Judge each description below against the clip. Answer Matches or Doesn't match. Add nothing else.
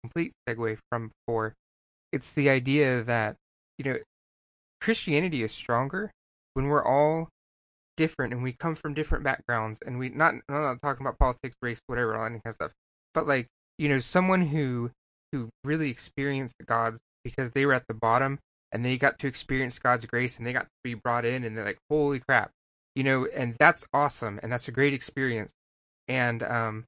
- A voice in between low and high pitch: Doesn't match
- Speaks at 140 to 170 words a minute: Doesn't match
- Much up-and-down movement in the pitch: Doesn't match